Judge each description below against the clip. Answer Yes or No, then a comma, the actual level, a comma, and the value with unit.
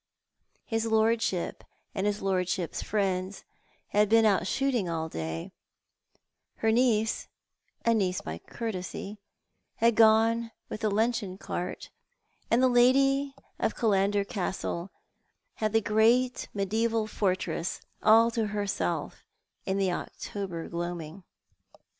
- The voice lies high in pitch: Yes, high, 210 Hz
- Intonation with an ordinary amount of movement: Yes, average, 3.5 semitones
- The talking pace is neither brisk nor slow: No, slow, 115 wpm